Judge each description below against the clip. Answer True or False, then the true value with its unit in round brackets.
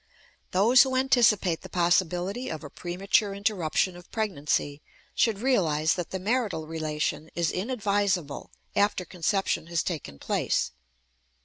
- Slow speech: True (125 wpm)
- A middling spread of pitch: True (4.4 semitones)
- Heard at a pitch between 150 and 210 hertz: True (185 Hz)